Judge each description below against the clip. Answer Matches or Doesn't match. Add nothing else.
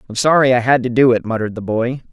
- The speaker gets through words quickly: Matches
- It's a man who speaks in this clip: Matches